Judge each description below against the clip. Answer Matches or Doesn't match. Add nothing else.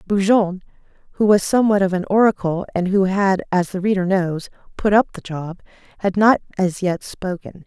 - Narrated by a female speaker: Matches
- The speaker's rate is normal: Matches